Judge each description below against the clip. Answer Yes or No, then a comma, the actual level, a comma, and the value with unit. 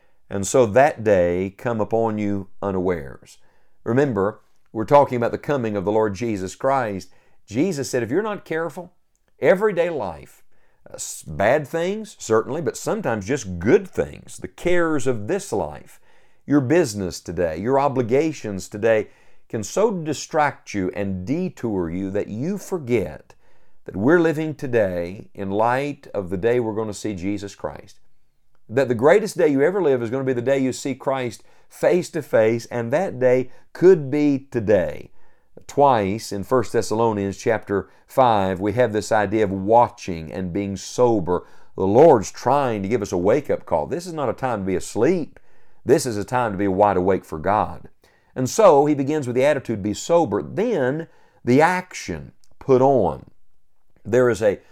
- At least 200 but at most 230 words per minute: No, average, 175 wpm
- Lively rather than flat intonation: Yes, wide, 6.0 semitones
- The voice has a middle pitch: No, low, 120 Hz